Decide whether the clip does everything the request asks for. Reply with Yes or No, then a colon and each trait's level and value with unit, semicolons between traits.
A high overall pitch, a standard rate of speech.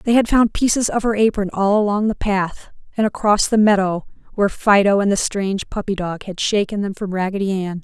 No: high, 205 Hz; fast, 215 wpm